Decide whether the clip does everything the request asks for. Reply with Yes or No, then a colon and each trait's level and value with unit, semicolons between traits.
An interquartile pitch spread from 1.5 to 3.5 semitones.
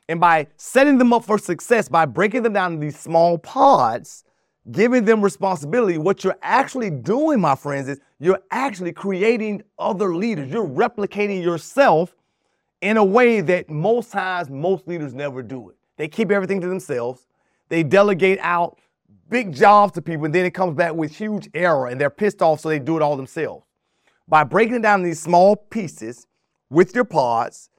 No: average, 4.6 semitones